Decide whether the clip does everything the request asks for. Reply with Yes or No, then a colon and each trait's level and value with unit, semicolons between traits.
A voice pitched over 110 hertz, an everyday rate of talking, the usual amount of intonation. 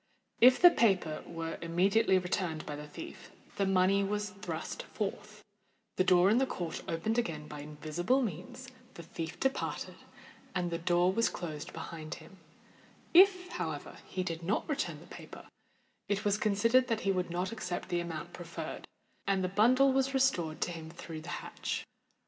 Yes: medium, 185 Hz; average, 170 wpm; average, 4.6 semitones